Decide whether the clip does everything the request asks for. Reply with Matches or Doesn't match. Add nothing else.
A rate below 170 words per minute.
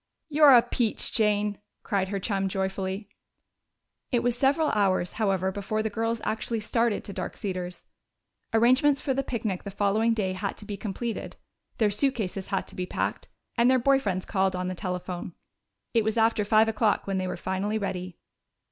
Doesn't match